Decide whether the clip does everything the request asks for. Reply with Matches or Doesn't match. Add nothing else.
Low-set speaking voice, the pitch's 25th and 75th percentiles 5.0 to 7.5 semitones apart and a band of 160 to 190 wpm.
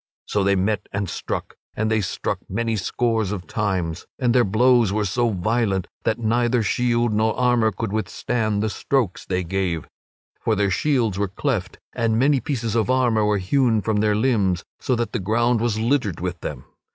Doesn't match